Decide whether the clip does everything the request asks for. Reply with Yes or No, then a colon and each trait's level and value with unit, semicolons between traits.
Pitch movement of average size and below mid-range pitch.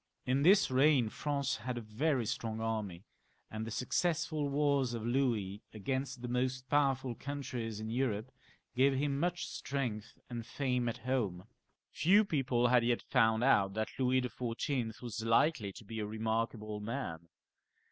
Yes: average, 3.6 semitones; low, 125 Hz